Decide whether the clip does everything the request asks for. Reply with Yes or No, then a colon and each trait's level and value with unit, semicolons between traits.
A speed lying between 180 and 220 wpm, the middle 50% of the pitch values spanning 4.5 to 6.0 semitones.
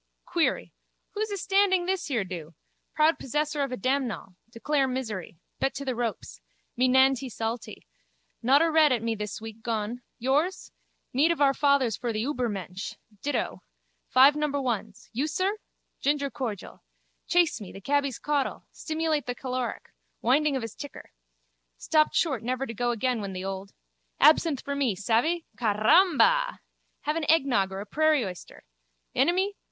No: average, 155 wpm; average, 5.1 semitones